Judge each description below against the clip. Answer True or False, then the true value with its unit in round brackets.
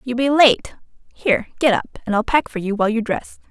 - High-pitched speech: True (235 Hz)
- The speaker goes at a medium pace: False (240 wpm)